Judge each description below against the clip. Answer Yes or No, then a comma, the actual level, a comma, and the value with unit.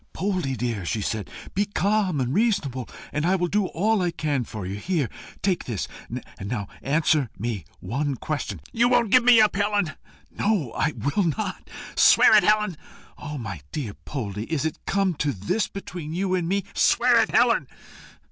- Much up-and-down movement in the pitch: Yes, wide, 8.1 semitones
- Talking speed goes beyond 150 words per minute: Yes, average, 180 wpm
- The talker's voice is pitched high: No, medium, 160 Hz